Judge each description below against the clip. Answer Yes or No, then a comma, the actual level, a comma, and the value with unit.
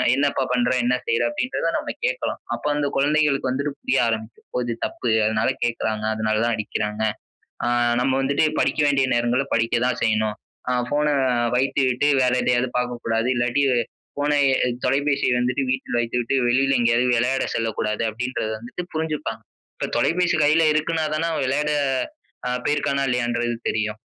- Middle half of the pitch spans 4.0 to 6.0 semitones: No, average, 3.6 semitones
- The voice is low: Yes, low, 125 Hz